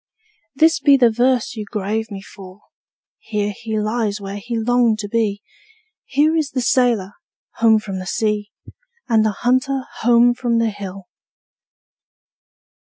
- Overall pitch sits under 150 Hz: No, high, 225 Hz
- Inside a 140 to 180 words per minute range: Yes, average, 145 wpm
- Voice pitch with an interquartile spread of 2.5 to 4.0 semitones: Yes, average, 2.9 semitones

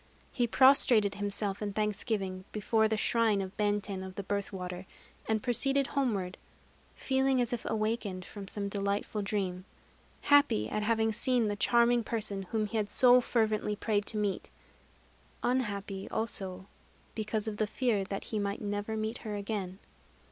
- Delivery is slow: No, average, 155 wpm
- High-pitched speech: Yes, high, 210 Hz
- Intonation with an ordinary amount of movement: No, narrow, 2.3 semitones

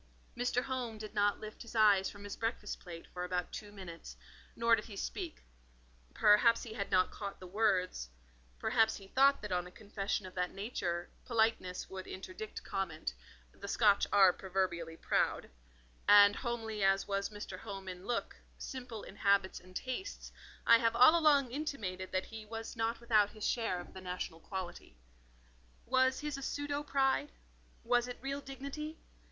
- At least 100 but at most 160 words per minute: No, average, 170 wpm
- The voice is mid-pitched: No, high, 210 Hz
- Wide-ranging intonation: No, average, 4.2 semitones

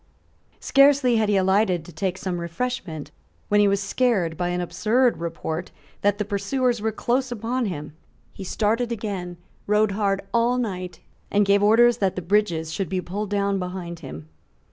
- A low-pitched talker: No, high, 200 Hz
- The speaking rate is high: No, average, 170 wpm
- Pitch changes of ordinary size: Yes, average, 4.1 semitones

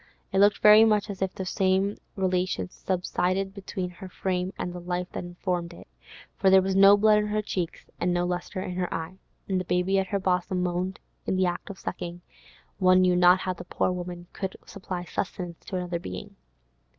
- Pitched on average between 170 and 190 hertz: Yes, medium, 185 Hz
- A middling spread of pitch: No, narrow, 1.4 semitones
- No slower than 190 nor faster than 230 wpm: Yes, average, 200 wpm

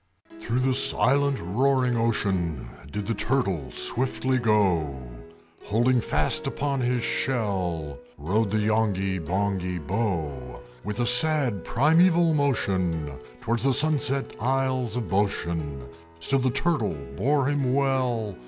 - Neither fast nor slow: No, slow, 120 wpm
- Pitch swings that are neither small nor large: No, wide, 6.1 semitones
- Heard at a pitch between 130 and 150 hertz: No, low, 115 Hz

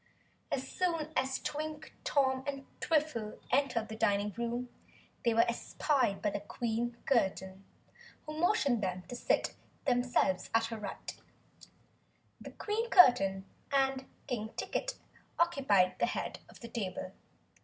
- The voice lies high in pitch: Yes, high, 245 Hz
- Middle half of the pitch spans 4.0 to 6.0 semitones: Yes, average, 4.7 semitones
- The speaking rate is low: Yes, slow, 125 wpm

